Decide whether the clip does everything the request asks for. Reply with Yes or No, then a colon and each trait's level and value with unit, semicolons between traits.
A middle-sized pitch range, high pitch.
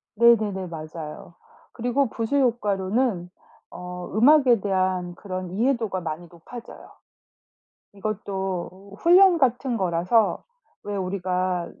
Yes: average, 4.6 semitones; high, 195 Hz